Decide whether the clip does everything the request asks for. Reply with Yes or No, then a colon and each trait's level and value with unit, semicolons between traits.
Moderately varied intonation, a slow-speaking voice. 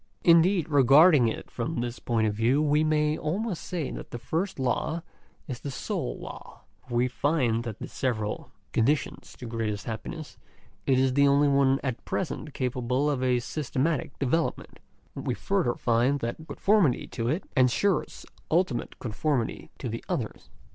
No: average, 4.5 semitones; average, 165 wpm